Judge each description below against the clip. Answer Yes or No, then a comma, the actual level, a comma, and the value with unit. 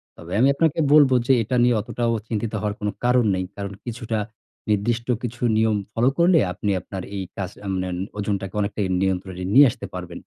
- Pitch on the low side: Yes, low, 105 Hz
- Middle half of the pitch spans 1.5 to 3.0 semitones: No, average, 4.0 semitones